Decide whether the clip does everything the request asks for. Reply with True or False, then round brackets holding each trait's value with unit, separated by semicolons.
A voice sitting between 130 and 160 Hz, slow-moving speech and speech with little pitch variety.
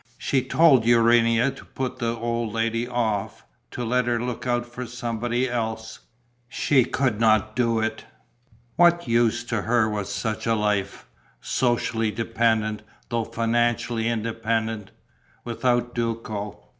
False (115 Hz; 130 wpm; 1.4 semitones)